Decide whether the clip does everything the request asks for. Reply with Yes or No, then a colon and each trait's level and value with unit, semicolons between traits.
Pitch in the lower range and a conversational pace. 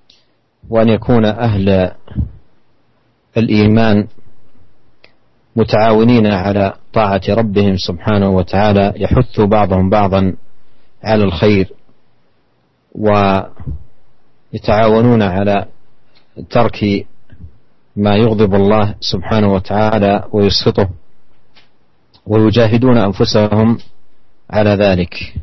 No: low, 105 Hz; slow, 65 wpm